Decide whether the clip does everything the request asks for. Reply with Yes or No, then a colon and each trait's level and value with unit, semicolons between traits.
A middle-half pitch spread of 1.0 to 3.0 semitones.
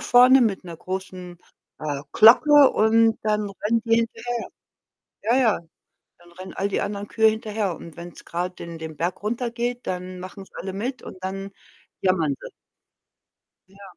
No: average, 3.9 semitones